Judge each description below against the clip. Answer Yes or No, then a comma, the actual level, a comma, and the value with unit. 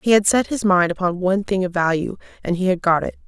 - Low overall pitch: No, medium, 185 Hz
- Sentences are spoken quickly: Yes, fast, 275 wpm